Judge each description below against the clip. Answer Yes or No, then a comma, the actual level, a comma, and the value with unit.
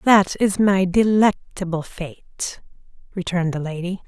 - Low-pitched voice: No, medium, 185 Hz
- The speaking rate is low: Yes, slow, 120 wpm